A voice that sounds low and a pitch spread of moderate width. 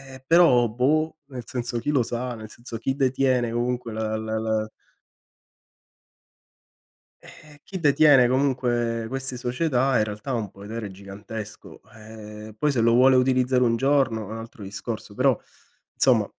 Yes: low, 120 Hz; average, 3.1 semitones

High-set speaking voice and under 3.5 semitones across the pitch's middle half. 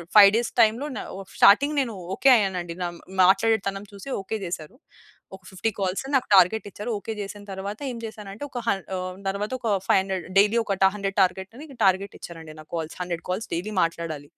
Yes: high, 195 Hz; average, 3.1 semitones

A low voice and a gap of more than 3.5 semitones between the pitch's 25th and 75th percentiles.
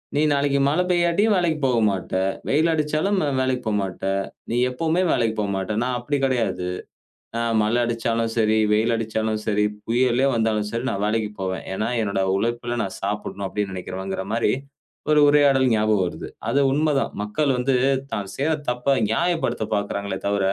Yes: low, 115 Hz; average, 5.0 semitones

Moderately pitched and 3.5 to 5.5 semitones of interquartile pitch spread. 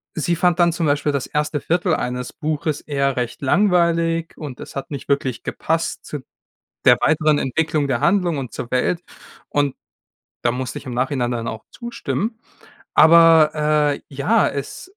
Yes: medium, 150 Hz; average, 3.8 semitones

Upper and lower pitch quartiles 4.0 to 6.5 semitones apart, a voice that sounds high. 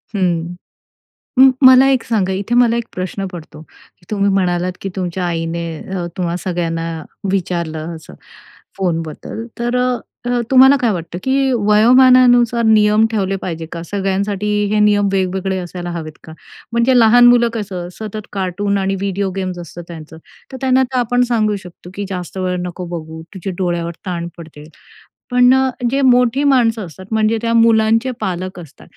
Yes: average, 4.8 semitones; high, 195 Hz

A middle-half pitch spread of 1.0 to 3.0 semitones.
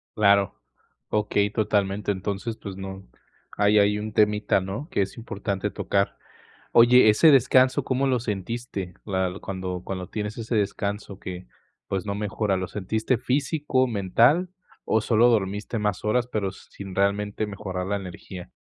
Yes: narrow, 2.5 semitones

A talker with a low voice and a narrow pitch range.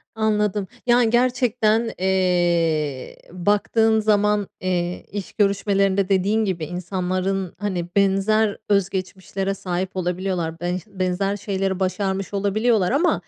No: high, 195 Hz; narrow, 2.3 semitones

